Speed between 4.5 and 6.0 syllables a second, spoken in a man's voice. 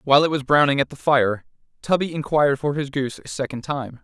No: 6.2 syllables/s; male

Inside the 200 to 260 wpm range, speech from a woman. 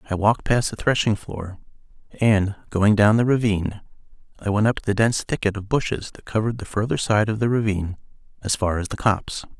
No: fast, 205 wpm; male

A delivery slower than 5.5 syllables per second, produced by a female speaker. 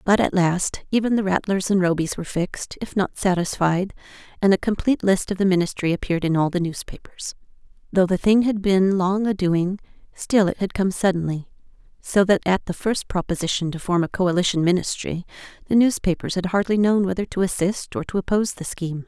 No: 5.8 syllables/s; female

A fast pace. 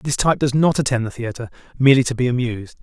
Yes: fast, 235 wpm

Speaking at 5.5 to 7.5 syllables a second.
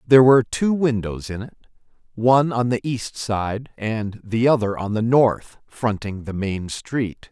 No: 4.2 syllables/s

